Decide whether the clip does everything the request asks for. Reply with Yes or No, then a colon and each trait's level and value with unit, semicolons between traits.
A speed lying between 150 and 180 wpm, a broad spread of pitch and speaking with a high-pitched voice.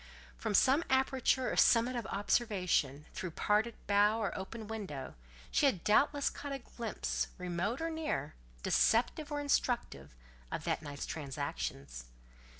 No: average, 140 wpm; wide, 7.2 semitones; high, 215 Hz